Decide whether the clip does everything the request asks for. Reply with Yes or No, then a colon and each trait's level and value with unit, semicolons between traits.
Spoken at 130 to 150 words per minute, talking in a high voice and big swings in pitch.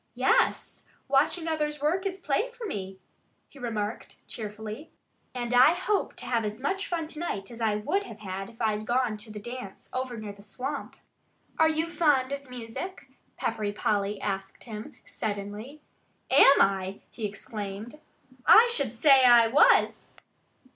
No: average, 160 wpm; high, 240 Hz; wide, 6.1 semitones